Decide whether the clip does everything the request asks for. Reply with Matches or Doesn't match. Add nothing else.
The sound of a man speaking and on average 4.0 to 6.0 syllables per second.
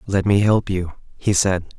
Matches